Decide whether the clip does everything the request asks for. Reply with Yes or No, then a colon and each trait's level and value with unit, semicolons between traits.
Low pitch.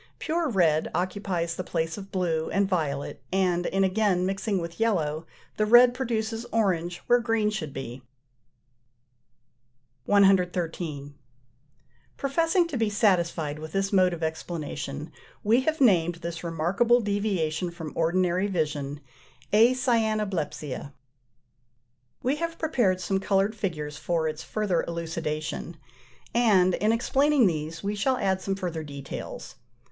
No: medium, 185 Hz